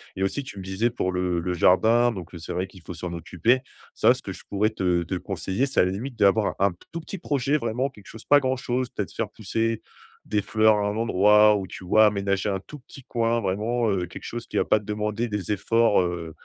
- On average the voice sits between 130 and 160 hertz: No, low, 105 Hz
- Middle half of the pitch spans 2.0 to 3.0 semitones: No, average, 3.9 semitones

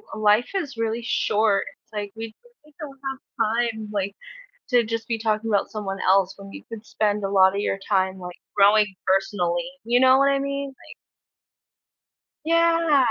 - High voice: Yes, high, 215 Hz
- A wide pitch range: No, average, 4.6 semitones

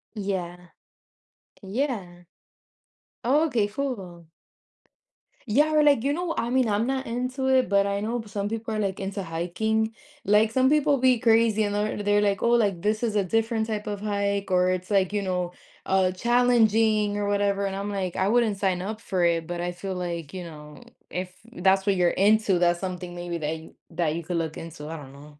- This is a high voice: Yes, high, 200 Hz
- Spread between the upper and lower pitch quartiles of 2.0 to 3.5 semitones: No, average, 3.9 semitones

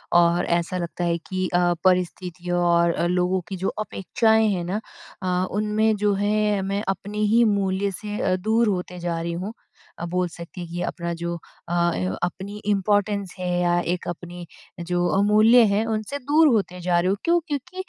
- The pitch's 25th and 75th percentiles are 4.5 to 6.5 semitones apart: No, average, 3.1 semitones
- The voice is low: No, medium, 185 Hz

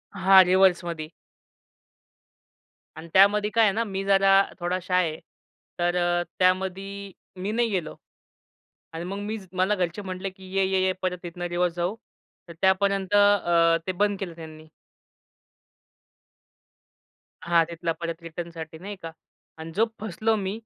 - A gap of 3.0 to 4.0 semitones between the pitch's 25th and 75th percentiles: No, narrow, 2.4 semitones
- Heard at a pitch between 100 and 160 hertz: No, medium, 185 Hz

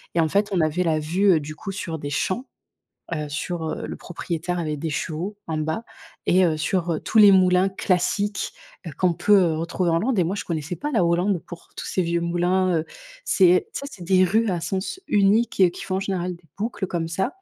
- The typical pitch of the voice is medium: Yes, medium, 180 Hz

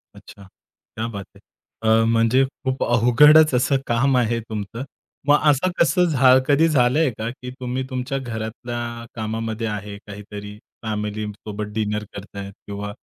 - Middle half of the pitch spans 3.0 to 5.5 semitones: Yes, average, 3.6 semitones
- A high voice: No, low, 115 Hz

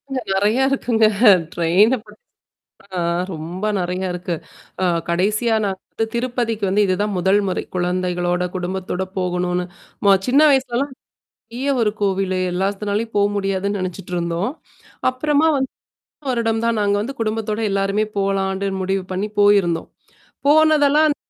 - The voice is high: Yes, high, 200 Hz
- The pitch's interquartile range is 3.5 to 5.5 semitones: Yes, average, 4.0 semitones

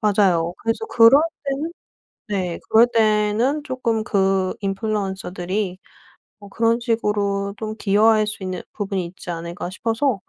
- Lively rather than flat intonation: No, average, 3.0 semitones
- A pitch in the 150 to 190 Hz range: No, high, 210 Hz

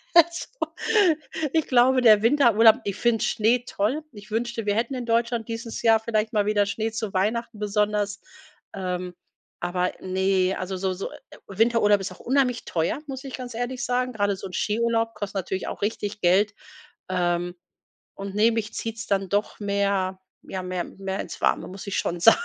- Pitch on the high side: Yes, high, 210 Hz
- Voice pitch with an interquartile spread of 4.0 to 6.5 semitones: No, average, 3.2 semitones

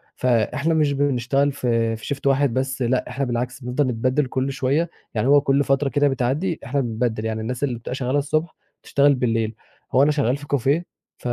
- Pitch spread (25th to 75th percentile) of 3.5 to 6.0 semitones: No, narrow, 2.6 semitones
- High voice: No, low, 135 Hz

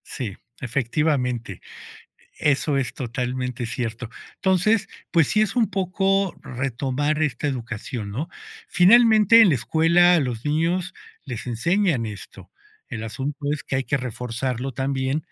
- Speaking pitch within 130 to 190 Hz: Yes, medium, 140 Hz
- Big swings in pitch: Yes, wide, 6.1 semitones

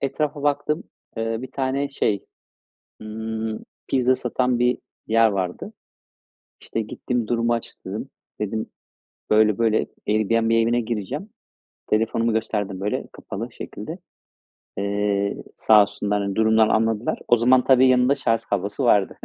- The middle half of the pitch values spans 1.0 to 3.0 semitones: Yes, average, 2.7 semitones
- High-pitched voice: No, low, 115 Hz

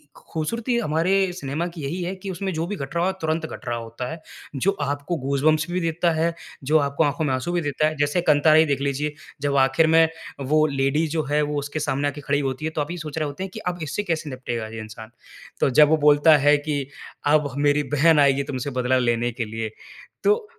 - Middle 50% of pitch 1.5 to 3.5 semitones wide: Yes, average, 2.8 semitones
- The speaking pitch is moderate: Yes, medium, 150 Hz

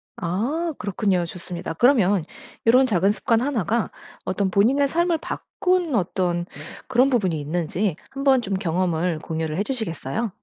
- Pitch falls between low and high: No, high, 200 Hz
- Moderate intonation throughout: No, wide, 6.6 semitones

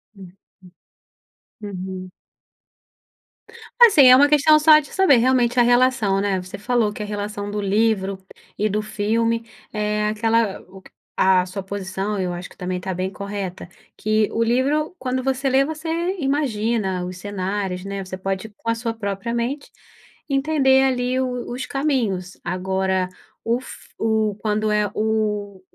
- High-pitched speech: Yes, high, 215 Hz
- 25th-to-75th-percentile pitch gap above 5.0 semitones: No, average, 4.5 semitones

